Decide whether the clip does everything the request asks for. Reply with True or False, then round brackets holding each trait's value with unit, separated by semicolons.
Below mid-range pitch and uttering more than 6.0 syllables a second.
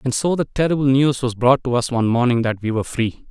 True (125 Hz; 6.4 syllables/s)